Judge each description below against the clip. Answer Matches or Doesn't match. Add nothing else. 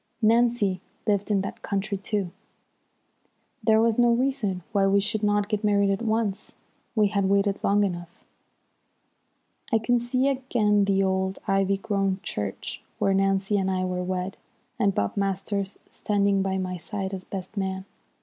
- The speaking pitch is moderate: Doesn't match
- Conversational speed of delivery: Matches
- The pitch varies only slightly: Matches